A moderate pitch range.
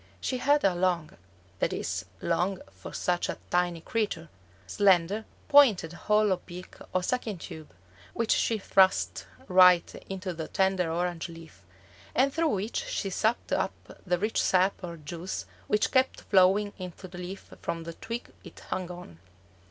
Yes: average, 3.4 semitones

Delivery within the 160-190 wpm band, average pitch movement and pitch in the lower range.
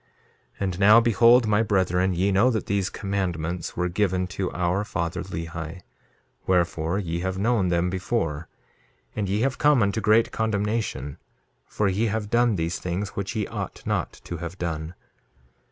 Yes: average, 165 wpm; average, 3.5 semitones; very low, 95 Hz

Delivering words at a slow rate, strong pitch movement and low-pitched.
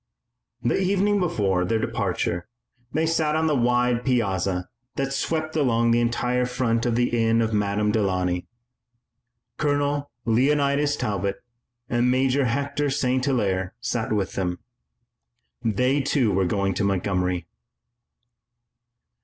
Yes: slow, 125 wpm; wide, 5.8 semitones; low, 120 Hz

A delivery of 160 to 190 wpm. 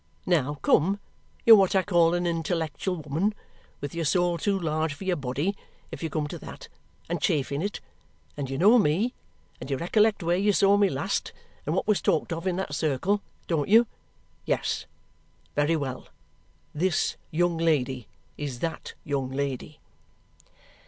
Yes: average, 165 wpm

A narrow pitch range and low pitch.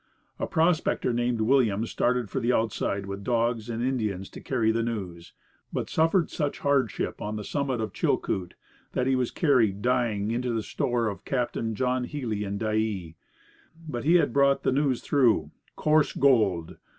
No: average, 3.7 semitones; low, 120 Hz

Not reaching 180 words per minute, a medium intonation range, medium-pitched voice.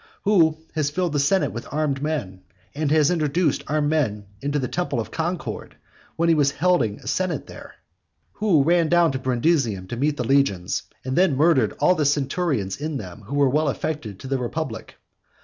No: average, 190 wpm; average, 3.9 semitones; medium, 145 Hz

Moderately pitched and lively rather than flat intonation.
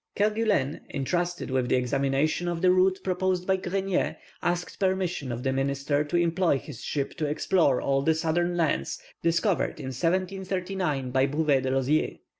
No: medium, 165 Hz; average, 5.0 semitones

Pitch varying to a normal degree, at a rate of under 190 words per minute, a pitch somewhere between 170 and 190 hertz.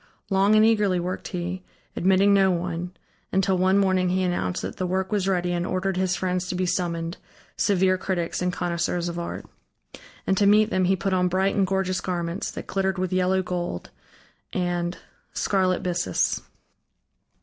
No: narrow, 1.4 semitones; average, 170 wpm; medium, 185 Hz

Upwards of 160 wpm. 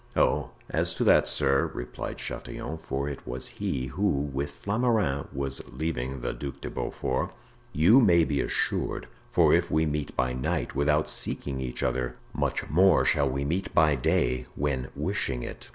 Yes: average, 170 wpm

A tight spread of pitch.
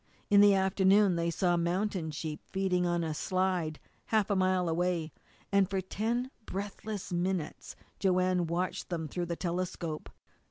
Yes: narrow, 2.1 semitones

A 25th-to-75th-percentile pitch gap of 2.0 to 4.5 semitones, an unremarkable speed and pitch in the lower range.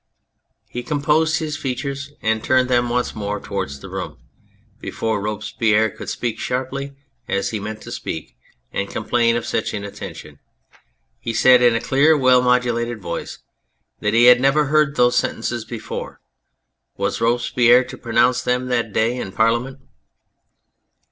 Yes: narrow, 2.6 semitones; average, 150 wpm; low, 120 Hz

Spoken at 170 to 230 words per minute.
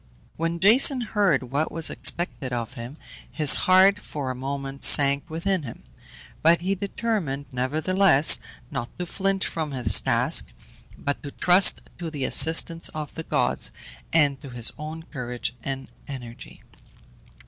No: average, 145 wpm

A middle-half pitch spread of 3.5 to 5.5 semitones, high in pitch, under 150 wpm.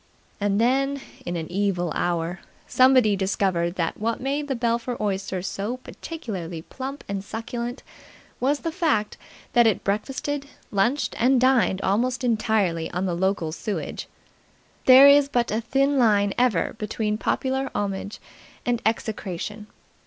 Yes: average, 4.8 semitones; high, 220 Hz; average, 140 wpm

